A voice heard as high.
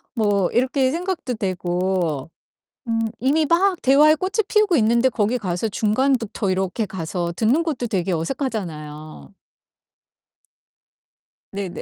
Yes: high, 220 Hz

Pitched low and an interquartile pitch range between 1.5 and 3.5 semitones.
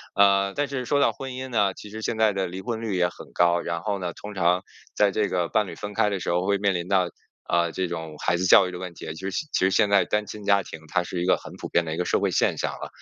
Yes: very low, 95 Hz; average, 2.9 semitones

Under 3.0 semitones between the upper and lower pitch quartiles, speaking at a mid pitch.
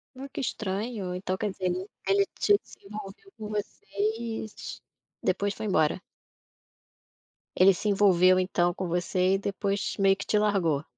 No: narrow, 2.4 semitones; high, 195 Hz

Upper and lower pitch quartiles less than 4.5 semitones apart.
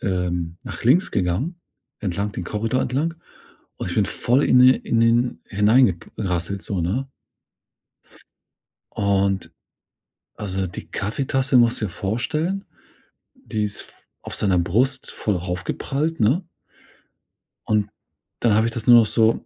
No: average, 4.8 semitones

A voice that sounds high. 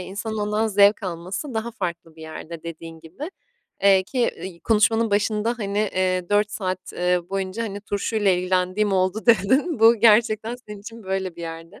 Yes: high, 200 Hz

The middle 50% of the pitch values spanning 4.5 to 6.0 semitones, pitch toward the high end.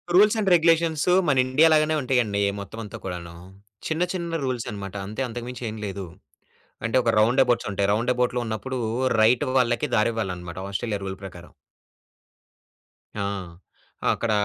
No: average, 4.9 semitones; low, 120 Hz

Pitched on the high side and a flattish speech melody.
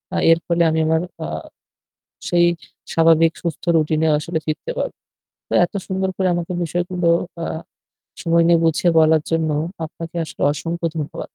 No: medium, 165 Hz; narrow, 1.5 semitones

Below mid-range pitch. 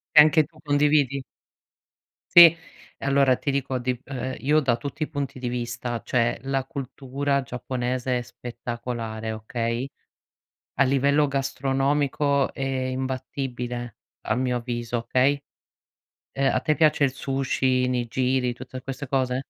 Yes: low, 130 Hz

